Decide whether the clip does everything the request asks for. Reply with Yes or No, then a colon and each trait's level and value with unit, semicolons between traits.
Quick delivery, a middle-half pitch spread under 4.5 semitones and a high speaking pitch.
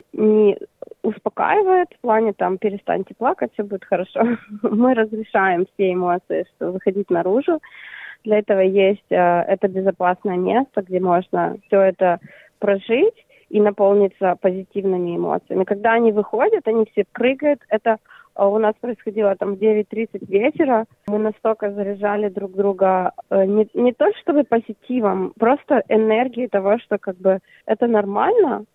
No: average, 140 wpm; average, 2.8 semitones; high, 210 Hz